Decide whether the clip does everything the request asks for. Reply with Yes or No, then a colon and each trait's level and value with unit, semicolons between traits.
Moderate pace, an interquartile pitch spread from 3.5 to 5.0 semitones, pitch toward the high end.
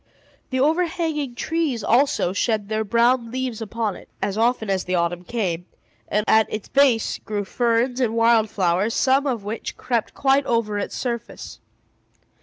Yes: average, 160 wpm; average, 3.8 semitones; high, 230 Hz